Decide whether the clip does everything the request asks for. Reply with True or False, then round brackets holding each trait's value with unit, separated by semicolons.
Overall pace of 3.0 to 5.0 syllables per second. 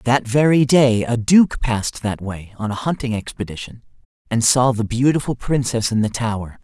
True (4.9 syllables/s)